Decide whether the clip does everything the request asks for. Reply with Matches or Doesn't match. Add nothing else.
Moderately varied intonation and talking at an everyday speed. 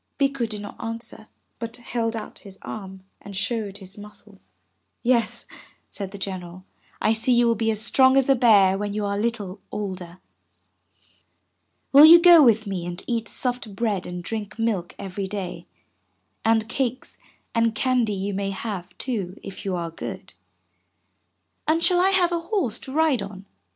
Matches